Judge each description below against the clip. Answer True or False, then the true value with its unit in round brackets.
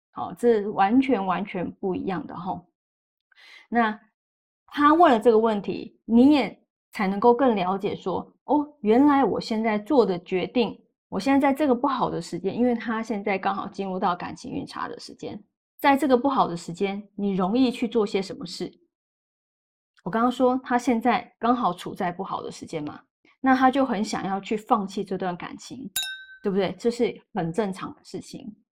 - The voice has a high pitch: True (230 Hz)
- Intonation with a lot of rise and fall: False (4.6 semitones)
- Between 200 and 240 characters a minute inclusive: False (260 characters per minute)